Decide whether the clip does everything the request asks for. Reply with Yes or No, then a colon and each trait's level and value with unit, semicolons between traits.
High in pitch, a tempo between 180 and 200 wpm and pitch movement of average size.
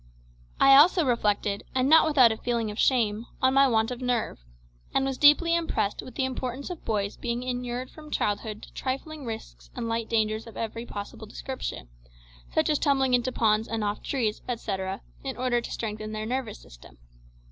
Yes: high, 240 Hz; average, 185 wpm; average, 3.5 semitones